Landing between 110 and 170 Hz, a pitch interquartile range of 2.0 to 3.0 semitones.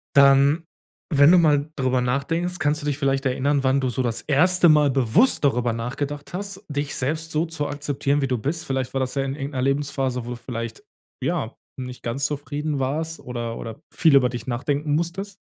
Yes: medium, 140 Hz; average, 2.7 semitones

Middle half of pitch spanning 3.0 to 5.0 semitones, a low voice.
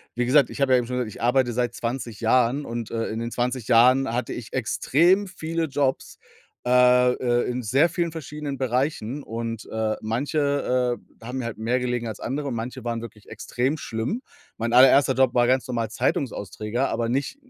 No: narrow, 2.6 semitones; low, 125 Hz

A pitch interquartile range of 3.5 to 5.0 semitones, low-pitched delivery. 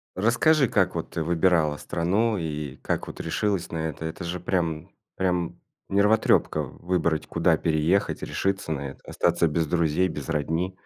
No: average, 3.1 semitones; very low, 85 Hz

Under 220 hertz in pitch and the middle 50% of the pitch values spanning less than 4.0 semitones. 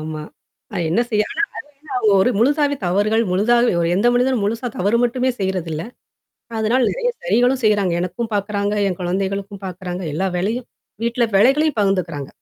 No: high, 205 Hz; average, 4.5 semitones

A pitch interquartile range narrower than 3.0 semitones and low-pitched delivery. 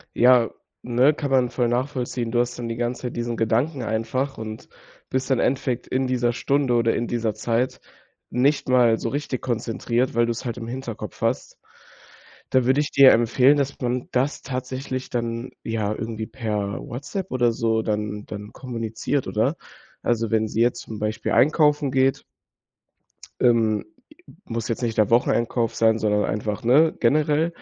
Yes: narrow, 2.5 semitones; low, 120 Hz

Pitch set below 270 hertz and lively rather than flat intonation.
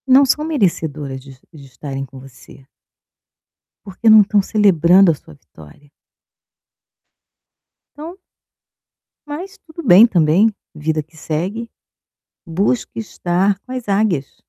Yes: medium, 185 Hz; wide, 7.3 semitones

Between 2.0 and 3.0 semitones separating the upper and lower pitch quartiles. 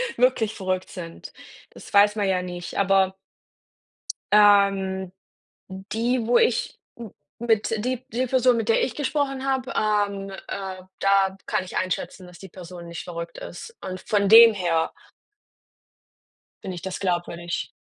No: average, 3.6 semitones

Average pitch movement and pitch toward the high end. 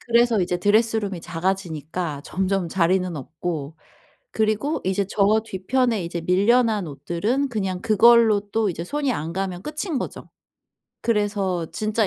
Yes: average, 4.2 semitones; high, 195 Hz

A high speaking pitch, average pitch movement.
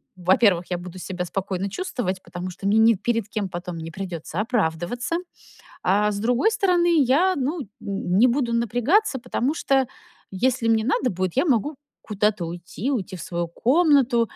No: high, 220 Hz; wide, 6.0 semitones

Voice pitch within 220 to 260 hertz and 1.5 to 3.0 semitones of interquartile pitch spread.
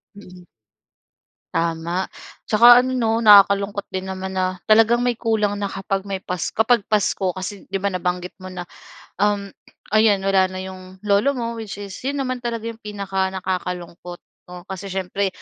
No: high, 195 Hz; narrow, 2.6 semitones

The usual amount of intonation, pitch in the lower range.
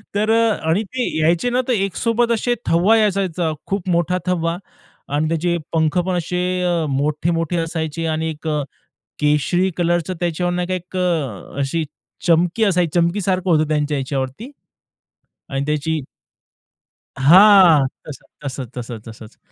No: average, 3.3 semitones; medium, 170 Hz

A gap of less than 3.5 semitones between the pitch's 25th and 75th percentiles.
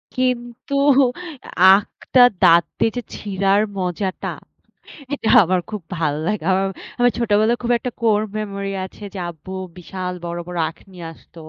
No: average, 3.8 semitones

